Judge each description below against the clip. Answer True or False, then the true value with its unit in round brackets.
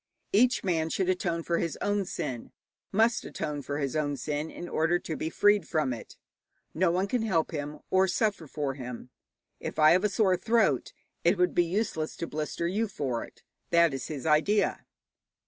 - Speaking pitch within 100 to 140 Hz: False (170 Hz)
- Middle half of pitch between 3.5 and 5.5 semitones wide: True (4.3 semitones)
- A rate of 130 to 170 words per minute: False (190 wpm)